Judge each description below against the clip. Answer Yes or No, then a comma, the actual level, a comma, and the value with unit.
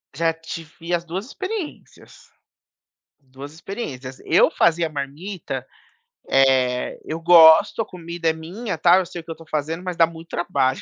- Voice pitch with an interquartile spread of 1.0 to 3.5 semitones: Yes, narrow, 2.5 semitones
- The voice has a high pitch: No, medium, 165 Hz